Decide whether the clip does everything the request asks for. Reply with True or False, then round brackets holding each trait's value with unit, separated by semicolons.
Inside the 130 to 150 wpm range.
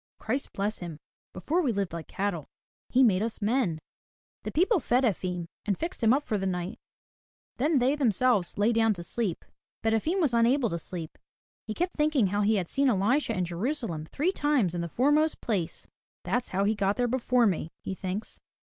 False (195 wpm)